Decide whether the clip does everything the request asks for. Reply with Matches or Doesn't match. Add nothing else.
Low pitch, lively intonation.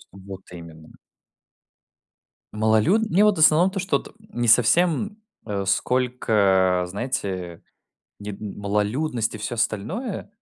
Matches